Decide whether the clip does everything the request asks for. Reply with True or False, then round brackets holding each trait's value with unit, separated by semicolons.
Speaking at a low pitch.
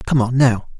True (125 Hz)